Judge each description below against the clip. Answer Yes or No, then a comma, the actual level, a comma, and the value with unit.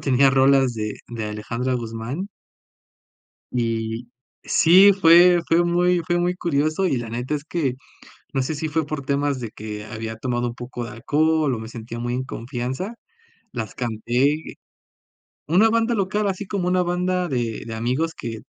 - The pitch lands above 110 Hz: Yes, low, 135 Hz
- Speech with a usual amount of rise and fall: No, wide, 6.7 semitones